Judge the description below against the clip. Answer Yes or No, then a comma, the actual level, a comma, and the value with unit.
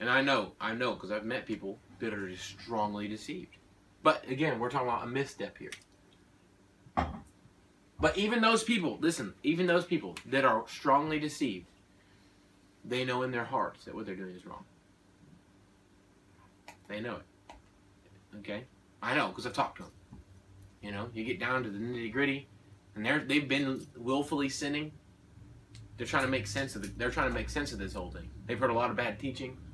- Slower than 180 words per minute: No, average, 190 wpm